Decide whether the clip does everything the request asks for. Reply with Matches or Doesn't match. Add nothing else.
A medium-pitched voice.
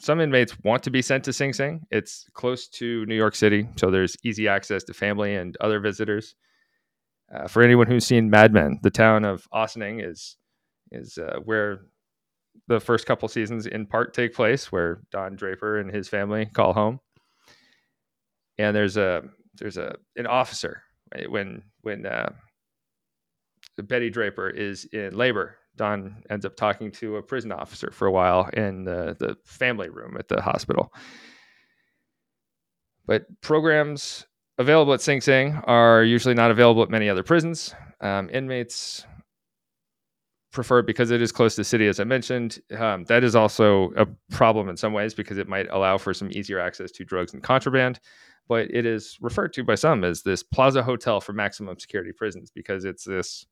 Doesn't match